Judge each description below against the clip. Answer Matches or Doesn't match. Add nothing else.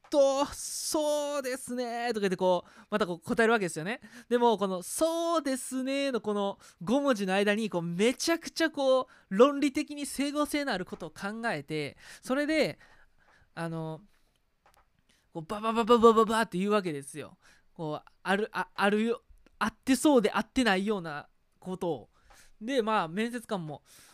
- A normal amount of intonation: Doesn't match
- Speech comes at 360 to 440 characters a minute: Doesn't match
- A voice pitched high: Matches